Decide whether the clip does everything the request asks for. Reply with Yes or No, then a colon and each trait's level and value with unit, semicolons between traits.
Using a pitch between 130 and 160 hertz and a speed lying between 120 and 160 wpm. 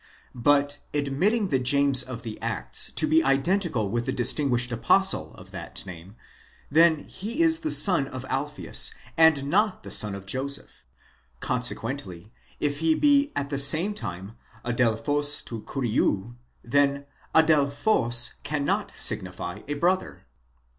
Yes: medium, 140 Hz; average, 140 wpm